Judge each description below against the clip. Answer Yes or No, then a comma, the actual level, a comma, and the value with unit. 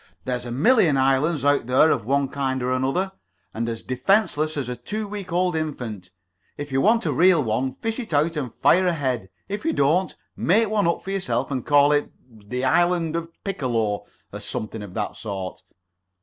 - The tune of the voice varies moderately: No, wide, 5.9 semitones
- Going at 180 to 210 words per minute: Yes, average, 190 wpm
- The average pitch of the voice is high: No, medium, 145 Hz